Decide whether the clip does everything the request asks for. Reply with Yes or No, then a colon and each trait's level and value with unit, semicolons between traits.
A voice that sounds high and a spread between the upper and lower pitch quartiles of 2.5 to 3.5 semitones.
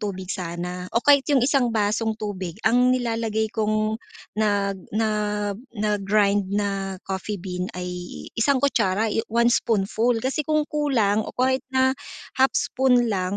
No: high, 215 Hz; average, 4.0 semitones